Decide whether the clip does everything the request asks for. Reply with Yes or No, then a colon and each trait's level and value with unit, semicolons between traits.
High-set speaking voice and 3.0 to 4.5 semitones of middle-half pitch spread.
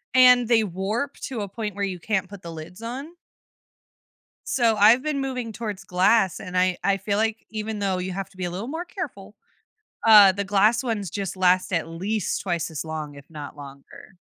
Yes: high, 200 Hz; average, 3.7 semitones